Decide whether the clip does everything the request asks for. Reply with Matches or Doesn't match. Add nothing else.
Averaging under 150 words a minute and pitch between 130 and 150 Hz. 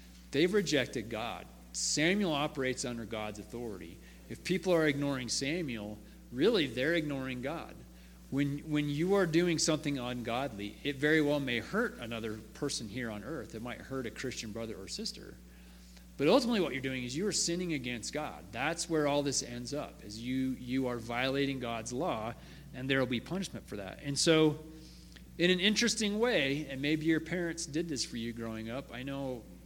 Doesn't match